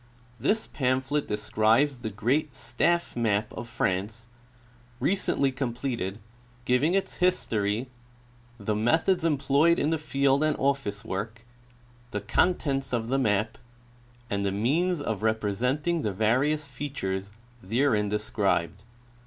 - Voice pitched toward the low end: Yes, low, 120 Hz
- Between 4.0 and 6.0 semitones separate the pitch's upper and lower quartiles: Yes, wide, 5.4 semitones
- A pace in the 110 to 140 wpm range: Yes, slow, 135 wpm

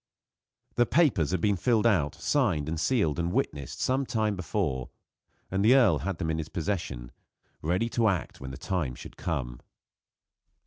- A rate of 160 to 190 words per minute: Yes, average, 165 wpm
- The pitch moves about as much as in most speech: No, wide, 6.1 semitones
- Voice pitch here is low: Yes, very low, 90 Hz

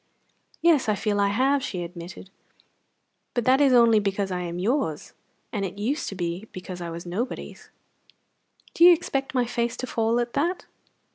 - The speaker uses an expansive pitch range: Yes, wide, 5.8 semitones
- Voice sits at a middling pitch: No, high, 220 Hz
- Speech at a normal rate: Yes, average, 180 wpm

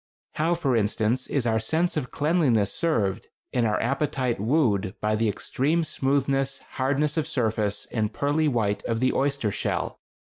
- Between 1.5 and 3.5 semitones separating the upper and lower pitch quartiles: No, average, 5.1 semitones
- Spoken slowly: No, average, 155 wpm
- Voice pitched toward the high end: No, low, 130 Hz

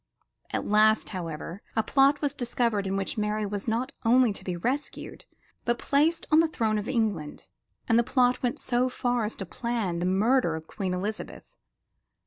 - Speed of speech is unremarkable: Yes, average, 180 wpm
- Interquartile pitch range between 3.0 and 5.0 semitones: Yes, average, 4.1 semitones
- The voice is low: No, high, 220 Hz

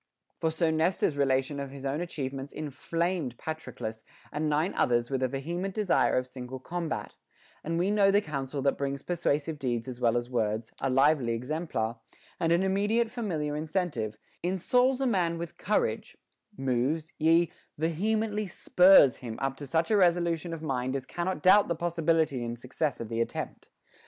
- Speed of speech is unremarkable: Yes, average, 170 wpm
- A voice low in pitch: No, medium, 155 Hz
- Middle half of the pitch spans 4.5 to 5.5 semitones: Yes, average, 4.8 semitones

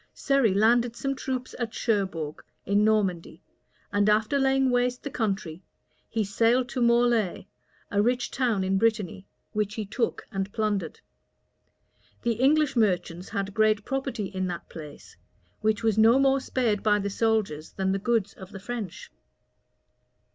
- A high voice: Yes, high, 215 Hz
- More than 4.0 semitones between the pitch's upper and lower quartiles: No, average, 3.7 semitones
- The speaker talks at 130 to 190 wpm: Yes, average, 150 wpm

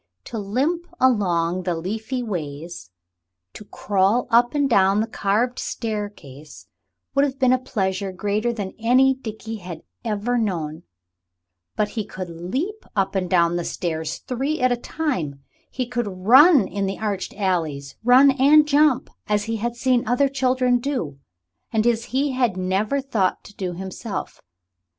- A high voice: Yes, high, 215 Hz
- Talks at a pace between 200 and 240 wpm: No, average, 155 wpm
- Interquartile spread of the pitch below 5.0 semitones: No, wide, 5.4 semitones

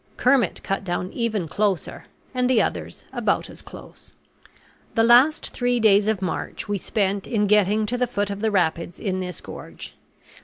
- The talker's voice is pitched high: Yes, high, 210 Hz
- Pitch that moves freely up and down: No, average, 3.4 semitones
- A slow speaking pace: No, average, 170 wpm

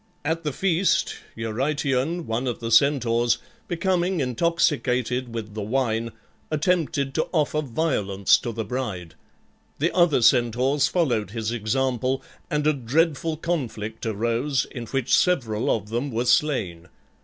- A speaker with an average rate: No, slow, 130 wpm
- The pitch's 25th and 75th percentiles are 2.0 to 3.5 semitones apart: No, average, 5.1 semitones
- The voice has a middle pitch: No, low, 130 Hz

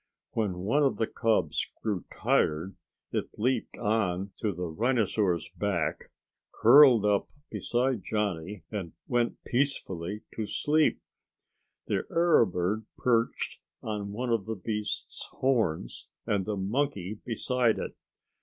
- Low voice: Yes, low, 105 Hz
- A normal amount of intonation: Yes, average, 3.9 semitones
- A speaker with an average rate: No, slow, 125 wpm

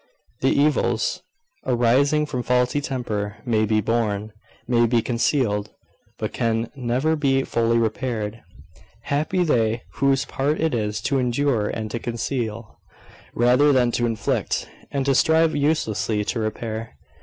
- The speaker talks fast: No, slow, 135 wpm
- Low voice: Yes, low, 120 Hz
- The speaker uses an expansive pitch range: No, average, 3.7 semitones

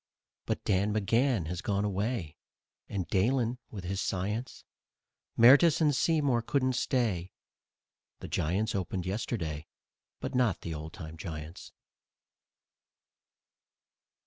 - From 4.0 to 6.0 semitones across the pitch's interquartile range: Yes, wide, 5.6 semitones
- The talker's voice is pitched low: Yes, low, 100 Hz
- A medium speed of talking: No, slow, 110 wpm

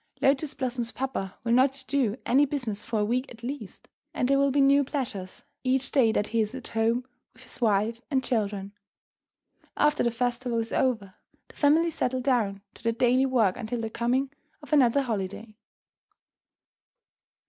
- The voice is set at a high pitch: Yes, high, 245 Hz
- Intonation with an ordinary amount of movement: Yes, average, 3.2 semitones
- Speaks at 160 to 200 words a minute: Yes, average, 170 wpm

